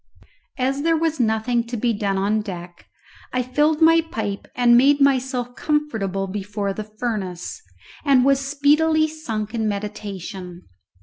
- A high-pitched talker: Yes, high, 240 Hz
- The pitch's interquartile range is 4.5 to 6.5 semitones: Yes, wide, 5.6 semitones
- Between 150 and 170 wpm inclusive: No, average, 140 wpm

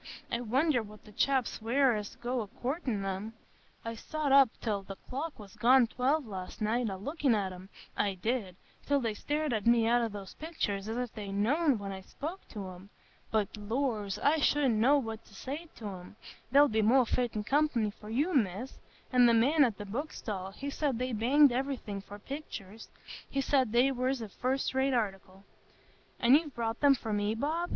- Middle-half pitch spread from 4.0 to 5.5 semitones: Yes, average, 4.8 semitones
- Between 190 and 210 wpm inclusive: Yes, average, 195 wpm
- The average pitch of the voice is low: No, high, 235 Hz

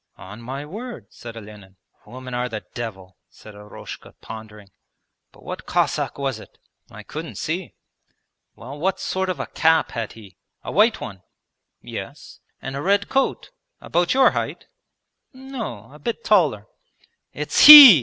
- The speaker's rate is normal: Yes, average, 150 wpm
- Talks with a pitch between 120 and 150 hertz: Yes, low, 135 Hz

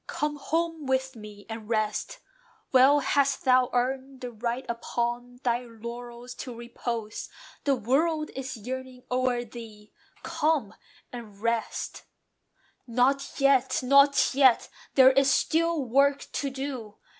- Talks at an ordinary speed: No, slow, 125 wpm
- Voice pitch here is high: Yes, very high, 255 Hz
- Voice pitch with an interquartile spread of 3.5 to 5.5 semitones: No, average, 2.7 semitones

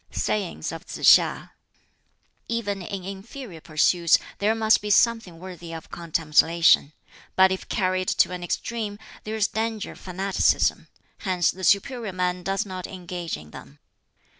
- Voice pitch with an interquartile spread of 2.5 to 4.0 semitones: Yes, average, 3.1 semitones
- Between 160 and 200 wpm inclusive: No, average, 145 wpm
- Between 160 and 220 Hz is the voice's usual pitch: Yes, medium, 185 Hz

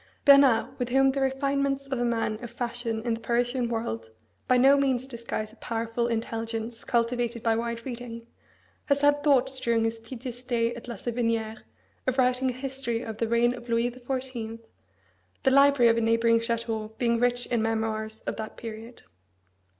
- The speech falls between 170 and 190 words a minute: Yes, average, 180 wpm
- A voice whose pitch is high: Yes, high, 235 Hz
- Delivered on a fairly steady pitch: Yes, narrow, 2.0 semitones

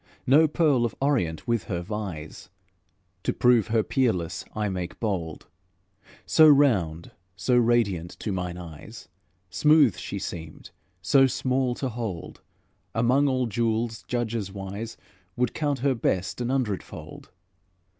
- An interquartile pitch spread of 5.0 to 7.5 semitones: Yes, wide, 5.6 semitones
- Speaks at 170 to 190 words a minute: No, slow, 135 wpm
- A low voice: Yes, low, 115 Hz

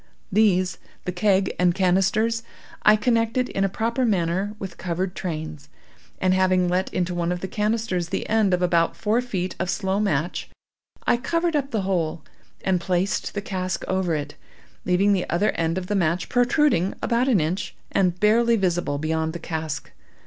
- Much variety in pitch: No, average, 3.5 semitones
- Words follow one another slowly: No, average, 170 wpm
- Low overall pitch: No, medium, 185 Hz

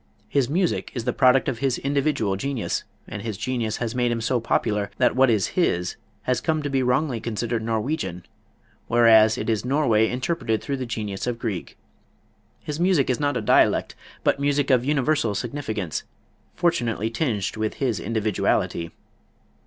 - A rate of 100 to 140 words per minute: No, average, 165 wpm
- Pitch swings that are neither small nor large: Yes, average, 4.0 semitones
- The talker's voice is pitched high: No, low, 120 Hz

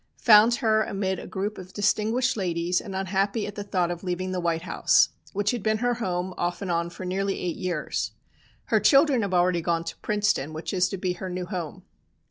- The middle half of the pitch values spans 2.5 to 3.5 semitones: Yes, average, 2.9 semitones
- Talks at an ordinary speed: No, fast, 215 wpm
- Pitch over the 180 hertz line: Yes, high, 190 Hz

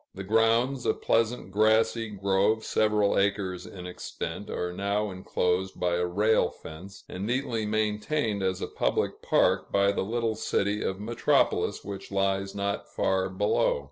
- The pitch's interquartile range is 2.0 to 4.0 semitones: Yes, narrow, 2.4 semitones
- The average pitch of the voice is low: Yes, low, 100 Hz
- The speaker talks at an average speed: Yes, average, 150 wpm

